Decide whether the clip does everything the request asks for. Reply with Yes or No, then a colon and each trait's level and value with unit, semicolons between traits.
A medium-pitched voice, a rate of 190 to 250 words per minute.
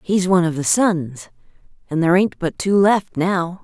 Yes: medium, 175 Hz; average, 200 wpm